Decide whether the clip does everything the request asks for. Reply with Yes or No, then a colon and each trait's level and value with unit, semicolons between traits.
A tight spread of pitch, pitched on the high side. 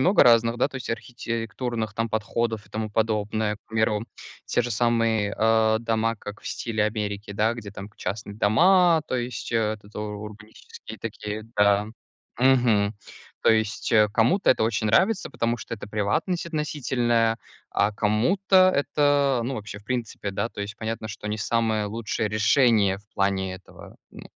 No: narrow, 2.2 semitones; low, 110 Hz